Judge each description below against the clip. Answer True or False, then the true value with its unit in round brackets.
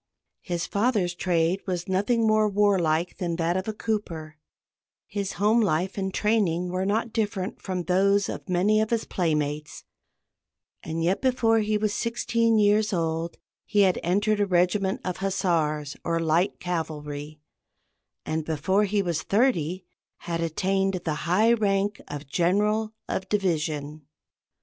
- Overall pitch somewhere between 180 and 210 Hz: True (185 Hz)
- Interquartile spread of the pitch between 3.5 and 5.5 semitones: True (3.9 semitones)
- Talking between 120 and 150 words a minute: True (145 wpm)